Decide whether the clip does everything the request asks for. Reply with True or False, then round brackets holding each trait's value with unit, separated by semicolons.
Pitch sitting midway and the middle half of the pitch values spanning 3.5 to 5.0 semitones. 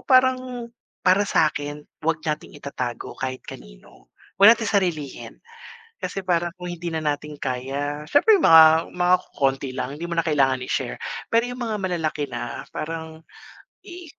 True (160 Hz; 4.7 semitones)